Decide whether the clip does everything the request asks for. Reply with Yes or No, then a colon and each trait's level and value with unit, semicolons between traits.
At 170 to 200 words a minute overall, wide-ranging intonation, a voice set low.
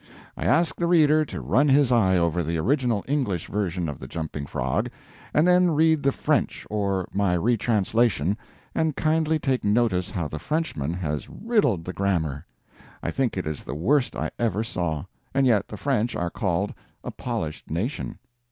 Yes: average, 175 wpm; wide, 8.4 semitones; low, 105 Hz